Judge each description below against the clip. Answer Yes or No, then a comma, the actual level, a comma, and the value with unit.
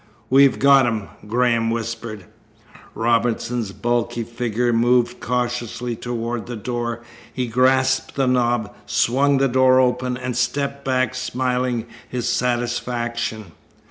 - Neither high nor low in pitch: No, low, 120 Hz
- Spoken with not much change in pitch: Yes, narrow, 1.5 semitones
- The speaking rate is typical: No, slow, 115 wpm